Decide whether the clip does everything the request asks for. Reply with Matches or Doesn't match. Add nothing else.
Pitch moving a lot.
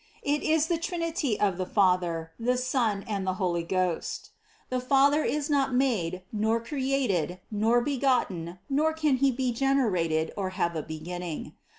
Matches